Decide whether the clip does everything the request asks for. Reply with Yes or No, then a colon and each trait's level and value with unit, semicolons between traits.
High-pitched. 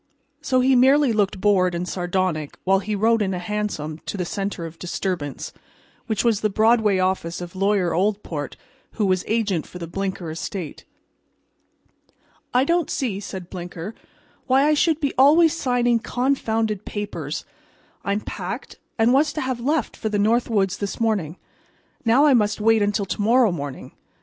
Yes: high, 205 Hz